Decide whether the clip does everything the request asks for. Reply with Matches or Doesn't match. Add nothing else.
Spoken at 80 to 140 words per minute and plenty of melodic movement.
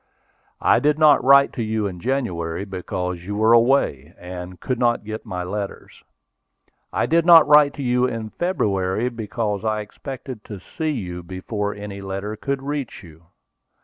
Doesn't match